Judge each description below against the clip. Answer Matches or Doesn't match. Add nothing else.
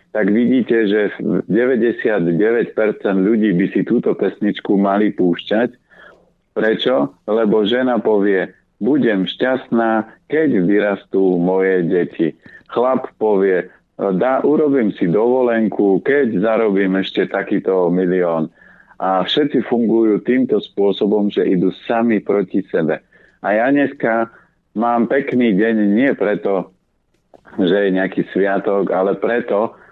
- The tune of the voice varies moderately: Matches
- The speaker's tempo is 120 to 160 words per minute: Doesn't match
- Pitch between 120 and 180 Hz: Doesn't match